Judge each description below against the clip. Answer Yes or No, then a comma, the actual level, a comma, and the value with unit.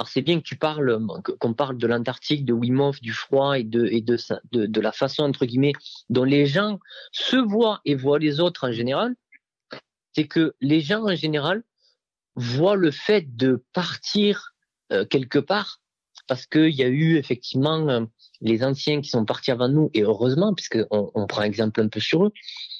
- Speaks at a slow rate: No, average, 190 wpm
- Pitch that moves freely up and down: Yes, wide, 6.1 semitones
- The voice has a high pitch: No, medium, 140 Hz